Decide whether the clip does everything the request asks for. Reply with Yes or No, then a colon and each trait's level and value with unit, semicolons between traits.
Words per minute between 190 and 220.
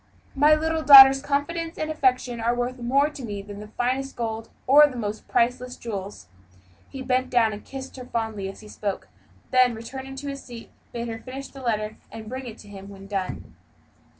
Yes: average, 200 wpm